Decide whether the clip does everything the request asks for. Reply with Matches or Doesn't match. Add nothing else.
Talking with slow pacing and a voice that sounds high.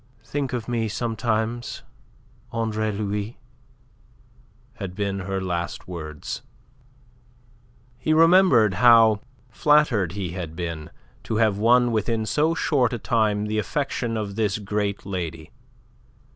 Doesn't match